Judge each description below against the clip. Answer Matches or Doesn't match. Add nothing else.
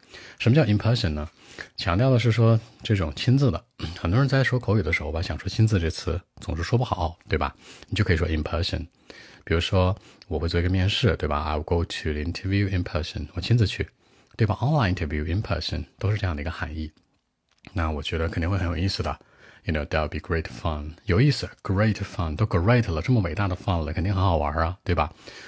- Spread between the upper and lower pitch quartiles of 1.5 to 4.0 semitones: Doesn't match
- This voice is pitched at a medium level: Doesn't match